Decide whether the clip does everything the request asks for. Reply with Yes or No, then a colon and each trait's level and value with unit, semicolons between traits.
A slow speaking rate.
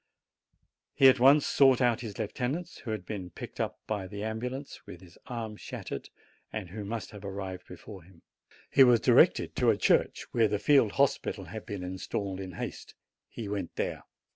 No: average, 185 wpm